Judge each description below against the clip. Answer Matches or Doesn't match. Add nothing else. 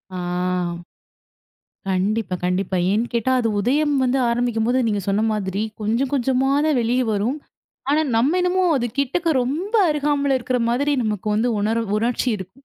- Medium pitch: Doesn't match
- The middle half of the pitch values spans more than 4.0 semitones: Matches